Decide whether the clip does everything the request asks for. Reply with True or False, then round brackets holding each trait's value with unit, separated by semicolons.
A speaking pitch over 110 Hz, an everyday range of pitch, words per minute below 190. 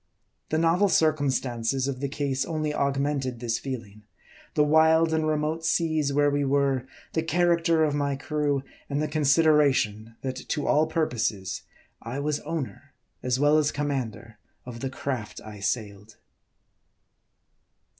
True (140 Hz; 3.4 semitones; 140 wpm)